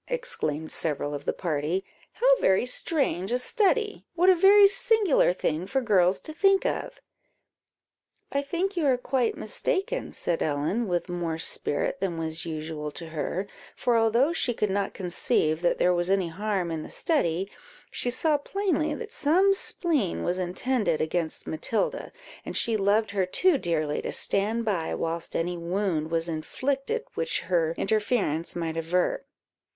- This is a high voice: Yes, high, 195 Hz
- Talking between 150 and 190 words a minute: Yes, average, 160 wpm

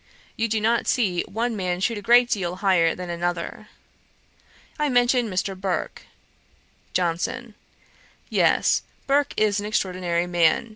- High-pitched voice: Yes, high, 200 Hz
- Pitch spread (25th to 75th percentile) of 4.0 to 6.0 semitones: Yes, average, 4.6 semitones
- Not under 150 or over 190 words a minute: No, slow, 135 wpm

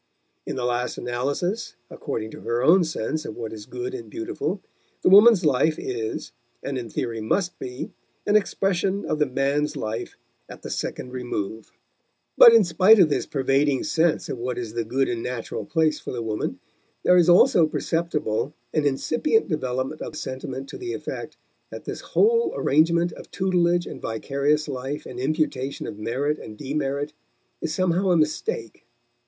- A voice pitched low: No, medium, 145 Hz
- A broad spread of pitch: Yes, wide, 5.7 semitones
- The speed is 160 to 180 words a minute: Yes, average, 170 wpm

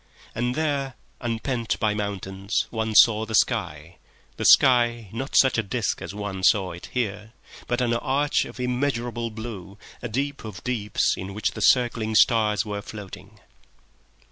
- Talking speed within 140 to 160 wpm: Yes, average, 150 wpm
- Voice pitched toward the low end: Yes, low, 110 Hz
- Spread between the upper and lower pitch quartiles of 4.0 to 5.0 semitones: No, average, 3.0 semitones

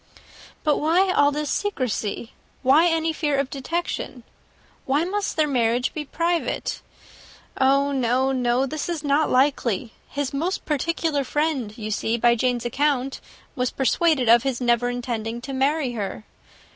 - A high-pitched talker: Yes, very high, 270 Hz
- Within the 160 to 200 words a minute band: No, average, 145 wpm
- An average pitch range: Yes, average, 3.8 semitones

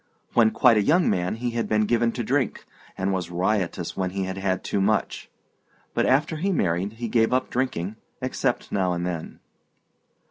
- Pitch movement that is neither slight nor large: Yes, average, 4.4 semitones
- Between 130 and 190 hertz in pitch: No, low, 105 Hz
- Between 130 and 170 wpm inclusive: No, average, 185 wpm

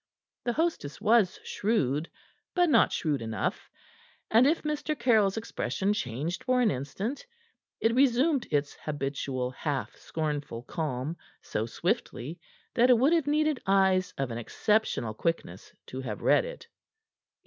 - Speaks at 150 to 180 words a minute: No, slow, 135 wpm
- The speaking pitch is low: No, high, 190 Hz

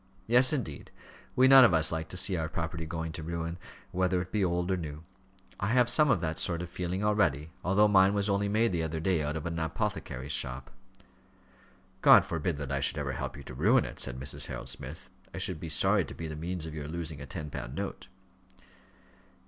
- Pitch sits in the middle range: No, very low, 85 Hz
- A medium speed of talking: No, fast, 220 wpm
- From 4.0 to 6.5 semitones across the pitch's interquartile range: No, average, 3.6 semitones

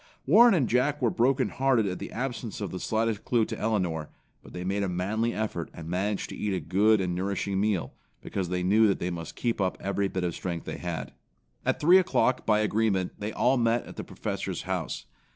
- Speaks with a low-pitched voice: Yes, low, 105 Hz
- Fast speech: Yes, fast, 220 wpm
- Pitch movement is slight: No, average, 4.2 semitones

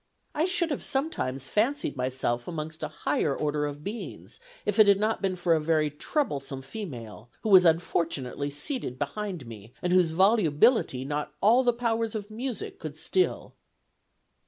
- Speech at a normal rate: Yes, average, 160 wpm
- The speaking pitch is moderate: Yes, medium, 165 Hz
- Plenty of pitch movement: Yes, wide, 7.3 semitones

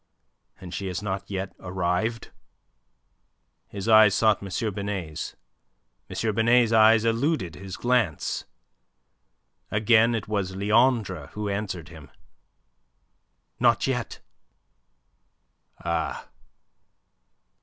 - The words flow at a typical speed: No, slow, 90 wpm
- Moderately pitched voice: No, low, 105 Hz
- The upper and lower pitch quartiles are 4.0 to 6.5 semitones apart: No, average, 3.2 semitones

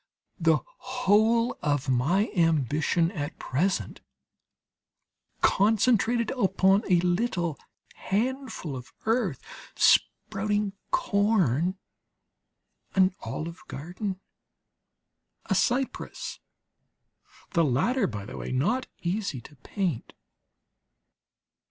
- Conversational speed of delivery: No, slow, 85 wpm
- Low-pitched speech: No, high, 190 Hz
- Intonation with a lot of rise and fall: Yes, wide, 5.9 semitones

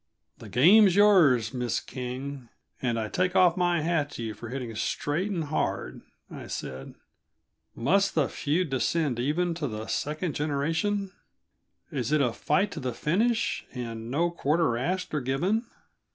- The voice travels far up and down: Yes, wide, 6.1 semitones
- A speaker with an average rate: Yes, average, 155 wpm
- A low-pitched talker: No, medium, 150 Hz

